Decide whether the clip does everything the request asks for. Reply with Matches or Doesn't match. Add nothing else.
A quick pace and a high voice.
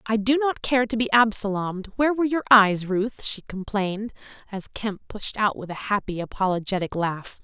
Doesn't match